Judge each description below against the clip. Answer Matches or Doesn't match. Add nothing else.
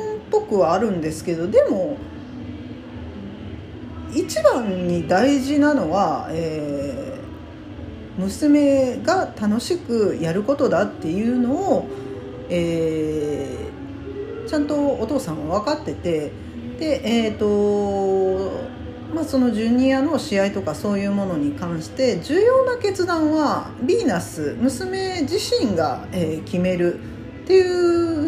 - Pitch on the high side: Matches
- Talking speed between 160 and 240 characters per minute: Matches